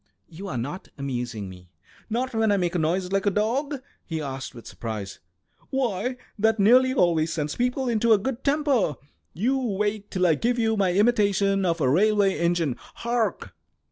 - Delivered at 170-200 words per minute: Yes, average, 175 wpm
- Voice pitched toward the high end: Yes, high, 200 Hz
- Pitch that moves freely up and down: Yes, wide, 6.3 semitones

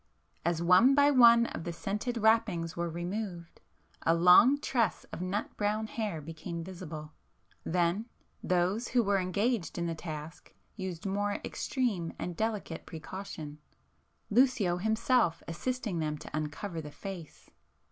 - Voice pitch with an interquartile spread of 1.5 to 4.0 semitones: No, average, 4.8 semitones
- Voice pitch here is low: No, medium, 185 Hz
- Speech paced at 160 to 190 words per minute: No, slow, 135 wpm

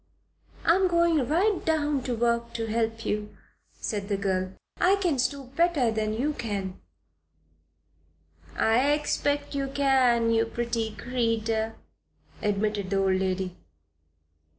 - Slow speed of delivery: Yes, slow, 125 wpm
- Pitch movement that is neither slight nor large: Yes, average, 4.8 semitones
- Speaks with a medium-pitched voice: No, high, 235 Hz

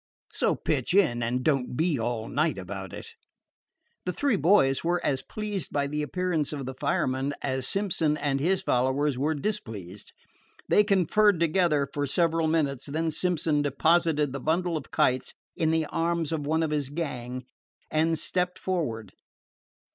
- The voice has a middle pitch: Yes, medium, 150 Hz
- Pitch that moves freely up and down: No, average, 4.3 semitones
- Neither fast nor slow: Yes, average, 160 wpm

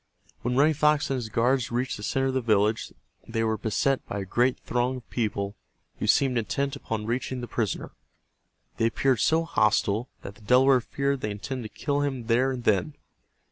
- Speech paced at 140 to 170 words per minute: No, average, 195 wpm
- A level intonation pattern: No, average, 3.4 semitones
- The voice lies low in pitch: Yes, low, 125 Hz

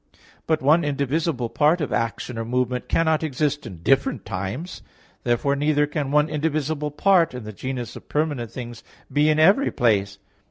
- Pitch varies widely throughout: No, average, 4.3 semitones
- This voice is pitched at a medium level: Yes, medium, 145 Hz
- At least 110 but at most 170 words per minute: Yes, average, 165 wpm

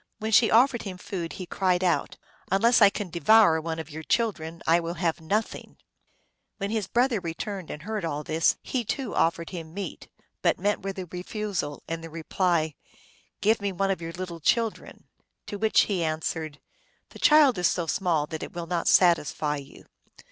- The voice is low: No, medium, 180 Hz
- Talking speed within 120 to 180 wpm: No, average, 200 wpm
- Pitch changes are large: No, average, 4.0 semitones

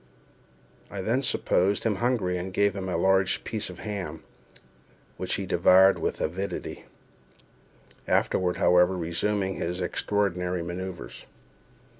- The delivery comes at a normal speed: No, slow, 115 wpm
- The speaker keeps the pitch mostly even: Yes, narrow, 2.3 semitones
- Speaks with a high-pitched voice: No, very low, 95 Hz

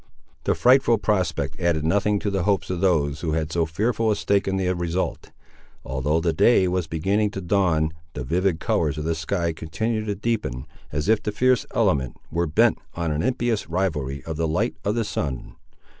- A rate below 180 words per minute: No, average, 195 wpm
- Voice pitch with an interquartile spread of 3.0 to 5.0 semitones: Yes, average, 4.6 semitones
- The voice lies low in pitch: Yes, very low, 85 Hz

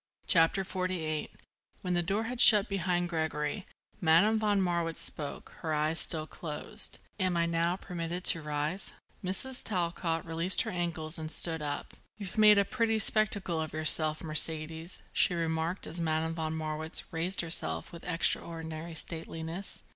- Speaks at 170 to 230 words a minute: No, average, 150 wpm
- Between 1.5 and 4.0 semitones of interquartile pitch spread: Yes, narrow, 2.5 semitones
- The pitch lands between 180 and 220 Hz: No, medium, 165 Hz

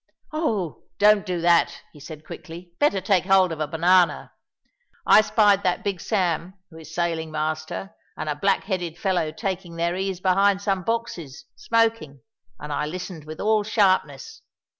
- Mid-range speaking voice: Yes, medium, 180 Hz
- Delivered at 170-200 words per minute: No, average, 160 wpm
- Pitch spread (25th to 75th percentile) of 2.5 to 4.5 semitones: Yes, average, 3.7 semitones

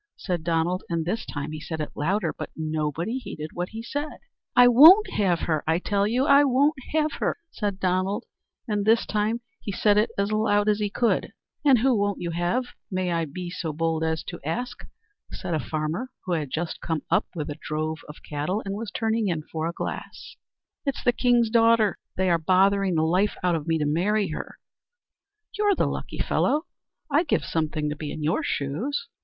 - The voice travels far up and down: Yes, wide, 5.9 semitones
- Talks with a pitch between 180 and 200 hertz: Yes, medium, 185 Hz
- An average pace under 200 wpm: No, fast, 205 wpm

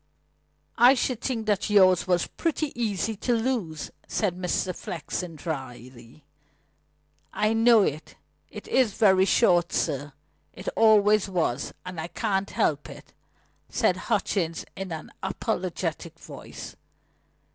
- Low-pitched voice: No, high, 190 Hz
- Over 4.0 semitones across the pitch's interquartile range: Yes, average, 4.9 semitones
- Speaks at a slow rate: Yes, slow, 125 wpm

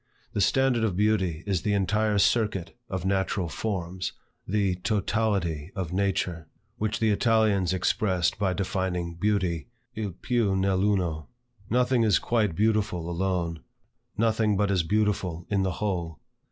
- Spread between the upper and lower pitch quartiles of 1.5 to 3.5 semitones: Yes, average, 3.2 semitones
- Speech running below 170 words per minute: Yes, average, 140 wpm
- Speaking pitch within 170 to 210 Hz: No, very low, 95 Hz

